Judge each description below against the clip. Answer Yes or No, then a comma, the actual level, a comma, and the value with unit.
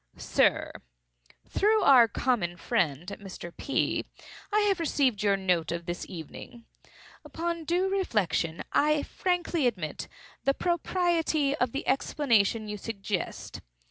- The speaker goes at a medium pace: No, slow, 115 wpm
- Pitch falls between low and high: No, high, 235 Hz